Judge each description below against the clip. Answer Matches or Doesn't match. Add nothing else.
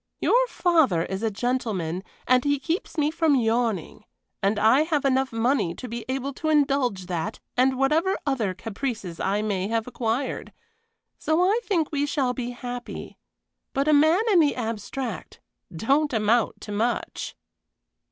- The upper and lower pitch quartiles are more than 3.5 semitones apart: Matches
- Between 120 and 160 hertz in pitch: Doesn't match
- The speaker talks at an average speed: Matches